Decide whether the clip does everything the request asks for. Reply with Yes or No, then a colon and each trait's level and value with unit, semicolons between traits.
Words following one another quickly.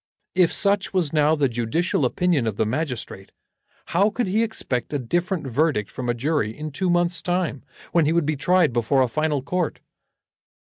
No: average, 185 wpm